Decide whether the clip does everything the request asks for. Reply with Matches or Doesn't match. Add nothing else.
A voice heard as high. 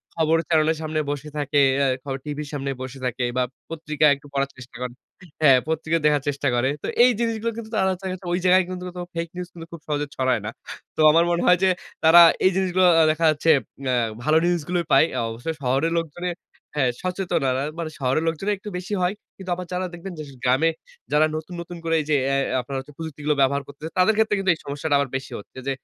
Doesn't match